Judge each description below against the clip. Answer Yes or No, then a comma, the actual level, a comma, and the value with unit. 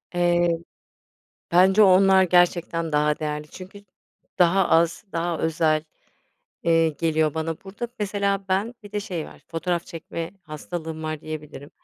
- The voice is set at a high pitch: No, medium, 170 Hz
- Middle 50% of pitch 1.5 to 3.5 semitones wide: Yes, average, 3.0 semitones